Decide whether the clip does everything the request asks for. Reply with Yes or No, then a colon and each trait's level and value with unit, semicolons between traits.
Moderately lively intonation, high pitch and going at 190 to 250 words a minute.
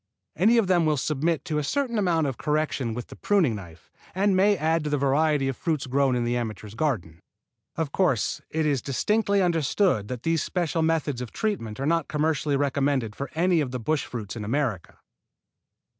No: average, 4.9 semitones; medium, 150 Hz; average, 195 wpm